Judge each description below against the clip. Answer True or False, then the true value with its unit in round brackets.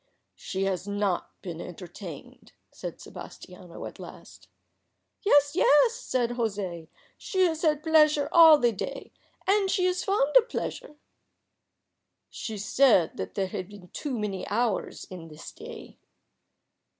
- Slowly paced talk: True (130 wpm)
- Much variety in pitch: True (8.8 semitones)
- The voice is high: True (230 Hz)